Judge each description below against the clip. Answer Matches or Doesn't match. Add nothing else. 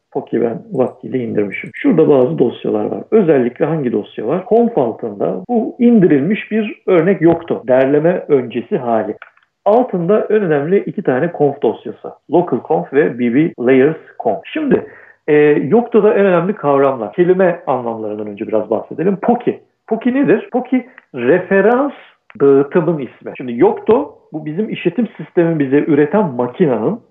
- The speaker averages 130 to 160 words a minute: Matches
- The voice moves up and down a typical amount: Doesn't match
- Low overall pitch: Doesn't match